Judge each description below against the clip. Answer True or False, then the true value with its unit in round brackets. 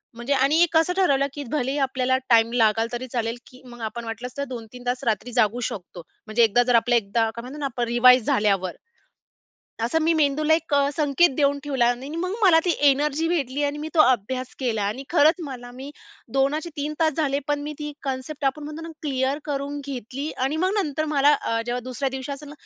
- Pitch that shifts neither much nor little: True (3.6 semitones)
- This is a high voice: True (270 Hz)